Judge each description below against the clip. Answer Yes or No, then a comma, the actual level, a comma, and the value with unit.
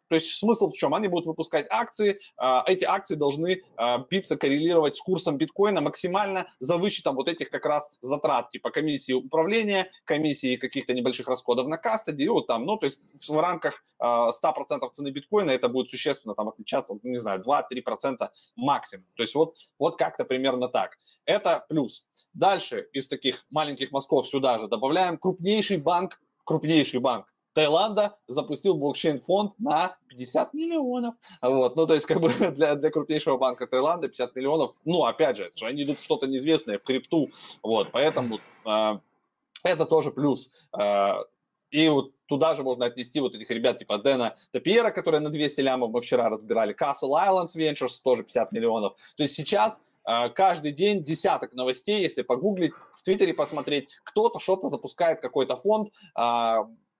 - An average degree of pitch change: No, wide, 6.1 semitones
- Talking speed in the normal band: No, fast, 165 wpm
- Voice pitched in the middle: Yes, medium, 150 Hz